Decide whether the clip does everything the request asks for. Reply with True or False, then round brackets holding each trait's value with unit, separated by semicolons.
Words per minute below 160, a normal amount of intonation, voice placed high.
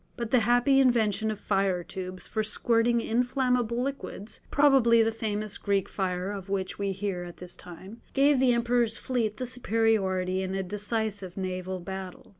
False (170 wpm; 3.9 semitones; 215 Hz)